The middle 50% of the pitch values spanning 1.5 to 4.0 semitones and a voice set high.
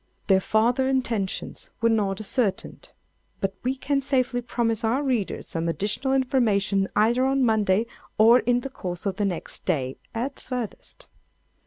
No: average, 4.5 semitones; high, 225 Hz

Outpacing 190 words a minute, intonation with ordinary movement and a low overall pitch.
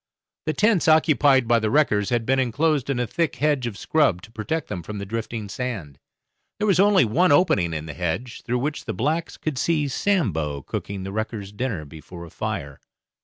No: average, 200 wpm; wide, 7.1 semitones; low, 120 Hz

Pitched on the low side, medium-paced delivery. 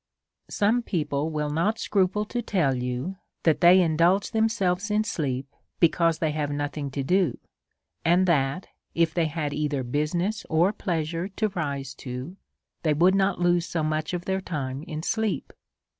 No: medium, 165 Hz; average, 160 wpm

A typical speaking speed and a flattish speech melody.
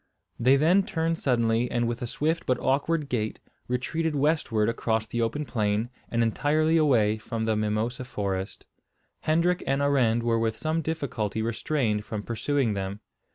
No: average, 155 wpm; average, 4.8 semitones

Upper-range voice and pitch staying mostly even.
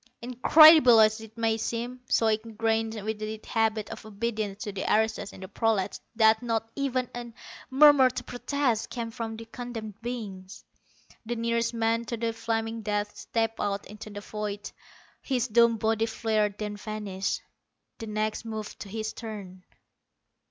Yes: high, 225 Hz; narrow, 1.6 semitones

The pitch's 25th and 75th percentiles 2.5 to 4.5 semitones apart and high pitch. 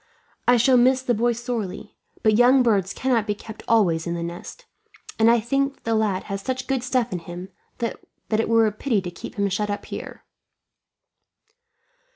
Yes: average, 3.8 semitones; high, 225 Hz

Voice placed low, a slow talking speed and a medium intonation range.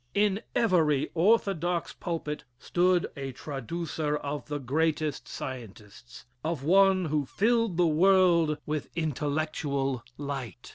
No: medium, 155 Hz; slow, 115 wpm; average, 3.9 semitones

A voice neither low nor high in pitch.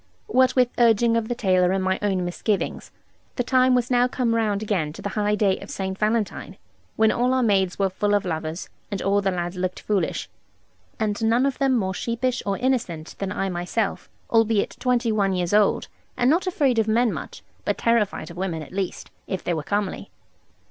No: high, 210 Hz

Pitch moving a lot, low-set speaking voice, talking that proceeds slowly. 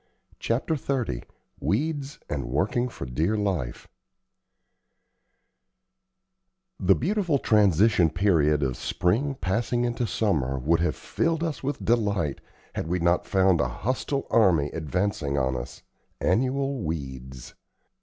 Yes: wide, 8.6 semitones; very low, 95 Hz; slow, 115 wpm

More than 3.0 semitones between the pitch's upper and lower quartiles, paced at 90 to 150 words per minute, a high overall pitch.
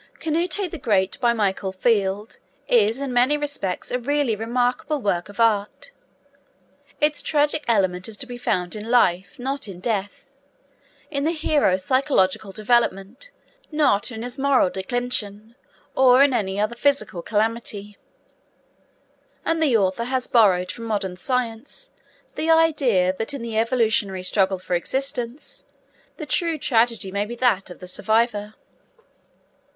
Yes: average, 5.0 semitones; average, 140 wpm; high, 230 Hz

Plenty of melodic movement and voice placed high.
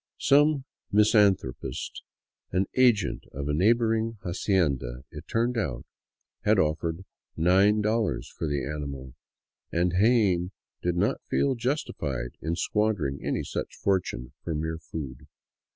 No: wide, 6.4 semitones; very low, 90 Hz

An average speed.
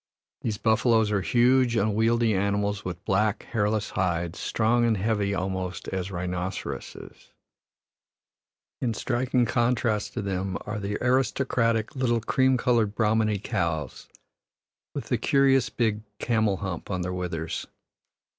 No: slow, 125 wpm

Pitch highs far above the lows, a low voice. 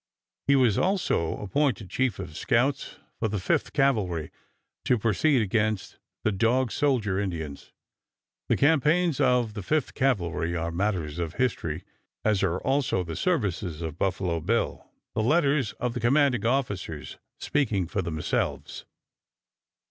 Yes: wide, 7.0 semitones; low, 110 Hz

